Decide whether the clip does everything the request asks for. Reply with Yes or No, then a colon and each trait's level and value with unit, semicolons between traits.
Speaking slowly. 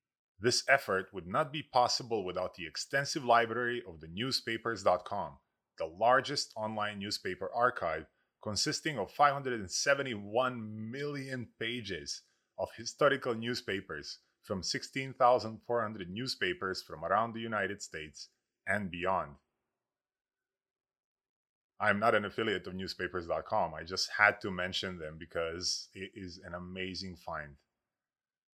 Yes: slow, 115 wpm